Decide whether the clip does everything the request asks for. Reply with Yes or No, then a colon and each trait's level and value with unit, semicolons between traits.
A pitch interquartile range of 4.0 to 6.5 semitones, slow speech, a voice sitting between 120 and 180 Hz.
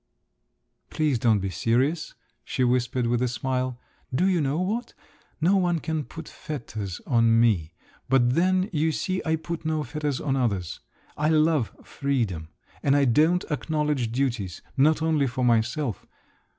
No: average, 5.0 semitones; average, 150 wpm; low, 135 Hz